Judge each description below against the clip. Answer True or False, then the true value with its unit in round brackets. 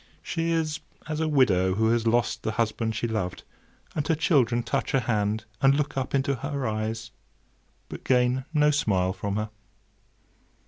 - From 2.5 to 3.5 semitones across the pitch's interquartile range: False (4.6 semitones)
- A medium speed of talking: True (170 wpm)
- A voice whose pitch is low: True (120 Hz)